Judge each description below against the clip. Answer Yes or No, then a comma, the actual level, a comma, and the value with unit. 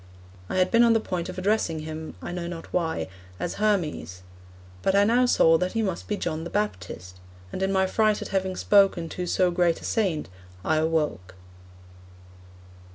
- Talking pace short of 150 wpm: No, average, 185 wpm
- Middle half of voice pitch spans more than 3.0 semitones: Yes, average, 3.8 semitones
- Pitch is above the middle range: No, medium, 180 Hz